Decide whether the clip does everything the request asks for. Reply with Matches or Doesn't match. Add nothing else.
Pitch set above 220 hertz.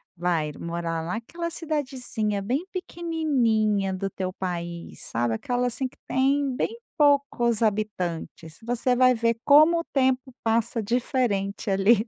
Matches